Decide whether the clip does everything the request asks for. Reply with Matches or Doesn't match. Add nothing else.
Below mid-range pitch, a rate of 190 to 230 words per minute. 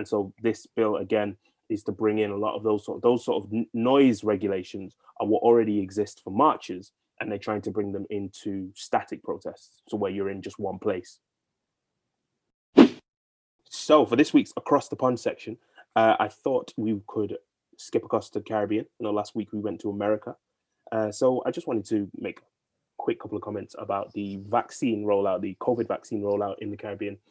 Matches